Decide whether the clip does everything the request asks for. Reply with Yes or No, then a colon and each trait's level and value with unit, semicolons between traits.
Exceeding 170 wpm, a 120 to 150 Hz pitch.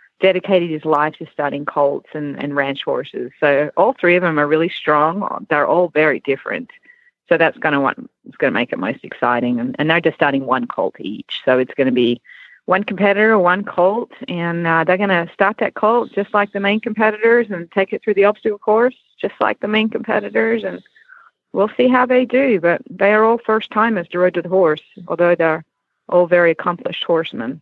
No: fast, 205 wpm; medium, 180 Hz